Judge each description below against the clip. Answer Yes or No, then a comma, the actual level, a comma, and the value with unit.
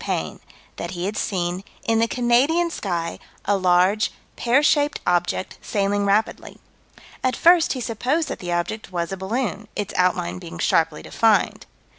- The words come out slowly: No, average, 155 wpm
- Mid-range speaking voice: No, high, 205 Hz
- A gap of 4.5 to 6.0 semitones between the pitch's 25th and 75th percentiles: Yes, average, 5.3 semitones